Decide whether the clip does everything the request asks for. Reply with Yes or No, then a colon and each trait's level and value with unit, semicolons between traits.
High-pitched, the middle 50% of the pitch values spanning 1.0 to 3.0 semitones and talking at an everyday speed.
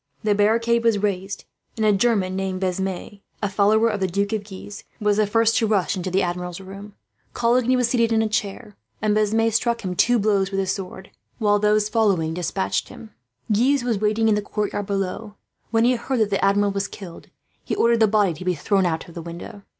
No: high, 205 Hz; narrow, 2.6 semitones; fast, 220 wpm